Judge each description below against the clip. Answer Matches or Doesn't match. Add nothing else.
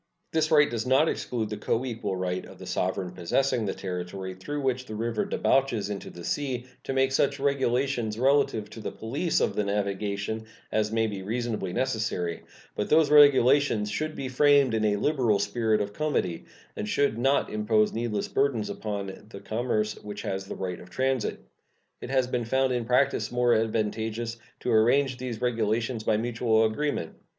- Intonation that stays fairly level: Doesn't match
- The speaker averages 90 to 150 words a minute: Doesn't match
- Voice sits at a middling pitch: Doesn't match